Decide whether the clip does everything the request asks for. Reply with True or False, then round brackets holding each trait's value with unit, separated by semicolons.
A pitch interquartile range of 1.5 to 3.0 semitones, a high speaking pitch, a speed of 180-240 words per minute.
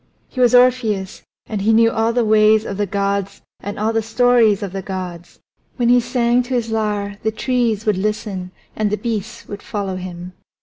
True (2.7 semitones; 215 Hz; 200 wpm)